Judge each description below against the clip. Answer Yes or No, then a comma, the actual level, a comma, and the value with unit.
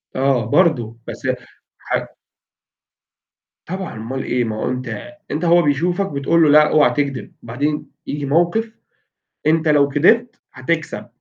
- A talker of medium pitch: Yes, medium, 150 Hz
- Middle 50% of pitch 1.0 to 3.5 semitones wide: No, average, 4.1 semitones